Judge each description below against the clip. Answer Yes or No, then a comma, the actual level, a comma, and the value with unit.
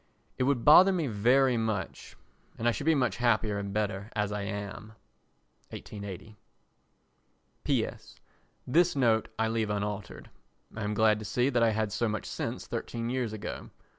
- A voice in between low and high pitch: No, low, 110 Hz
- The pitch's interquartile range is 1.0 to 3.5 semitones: Yes, average, 2.9 semitones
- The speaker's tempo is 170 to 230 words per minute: No, average, 160 wpm